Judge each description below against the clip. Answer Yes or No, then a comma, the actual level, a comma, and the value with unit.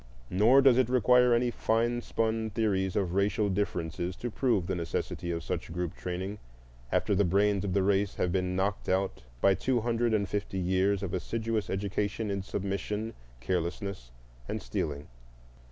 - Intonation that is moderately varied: Yes, average, 3.3 semitones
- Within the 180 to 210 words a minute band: No, average, 165 wpm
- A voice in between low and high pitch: No, low, 100 Hz